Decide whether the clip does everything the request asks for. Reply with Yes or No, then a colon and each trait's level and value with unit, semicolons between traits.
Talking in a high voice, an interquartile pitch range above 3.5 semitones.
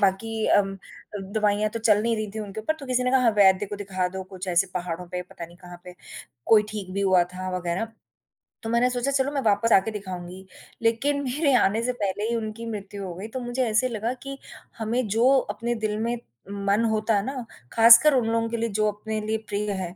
No: high, 215 Hz; average, 3.2 semitones